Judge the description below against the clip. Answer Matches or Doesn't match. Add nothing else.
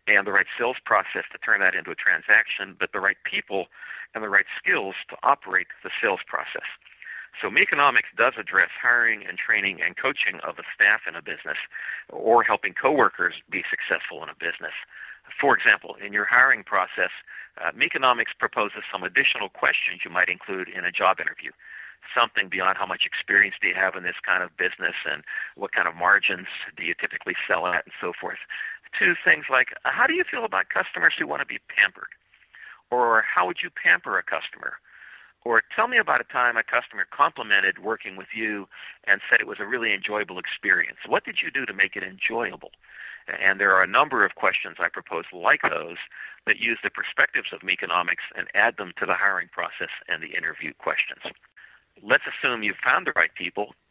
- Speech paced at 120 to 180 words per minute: Doesn't match